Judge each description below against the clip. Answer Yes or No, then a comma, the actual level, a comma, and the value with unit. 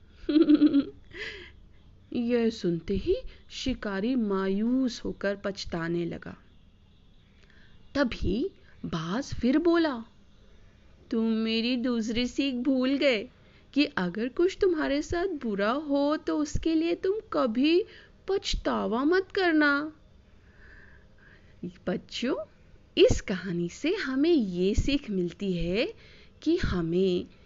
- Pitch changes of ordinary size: No, wide, 8.1 semitones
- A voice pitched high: Yes, very high, 255 Hz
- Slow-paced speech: Yes, slow, 95 wpm